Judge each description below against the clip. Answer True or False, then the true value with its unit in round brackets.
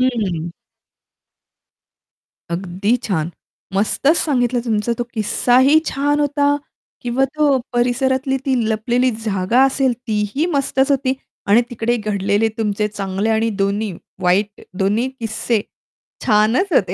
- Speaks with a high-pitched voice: True (230 Hz)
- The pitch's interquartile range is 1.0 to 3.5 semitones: False (4.2 semitones)